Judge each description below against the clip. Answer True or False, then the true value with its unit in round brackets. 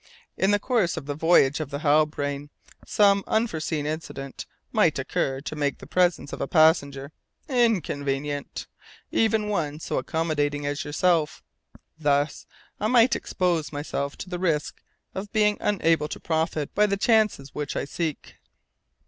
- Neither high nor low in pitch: True (155 Hz)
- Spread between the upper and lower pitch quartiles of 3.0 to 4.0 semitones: False (5.2 semitones)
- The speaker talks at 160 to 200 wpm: False (150 wpm)